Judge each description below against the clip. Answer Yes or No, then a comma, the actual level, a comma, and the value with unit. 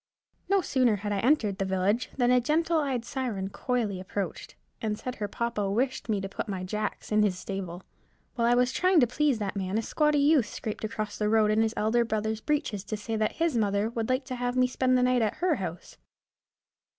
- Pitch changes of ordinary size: Yes, average, 3.7 semitones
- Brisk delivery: Yes, fast, 225 wpm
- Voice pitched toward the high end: Yes, high, 225 Hz